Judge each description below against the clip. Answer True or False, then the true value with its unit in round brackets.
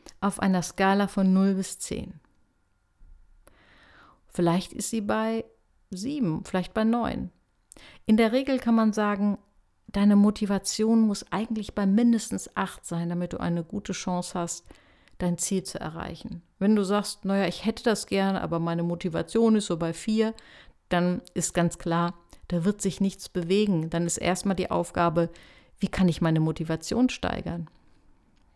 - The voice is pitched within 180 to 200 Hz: True (190 Hz)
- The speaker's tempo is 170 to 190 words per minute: False (155 wpm)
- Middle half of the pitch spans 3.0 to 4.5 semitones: True (3.6 semitones)